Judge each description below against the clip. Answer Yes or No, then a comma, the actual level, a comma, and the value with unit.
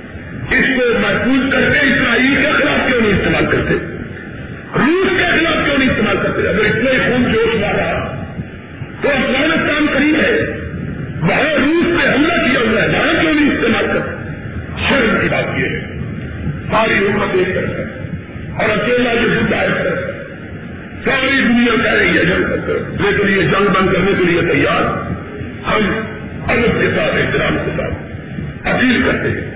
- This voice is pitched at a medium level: No, high, 240 Hz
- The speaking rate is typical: Yes, average, 155 wpm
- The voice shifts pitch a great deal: Yes, wide, 5.7 semitones